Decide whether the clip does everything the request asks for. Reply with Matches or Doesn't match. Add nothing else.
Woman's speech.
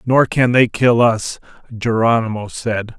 Doesn't match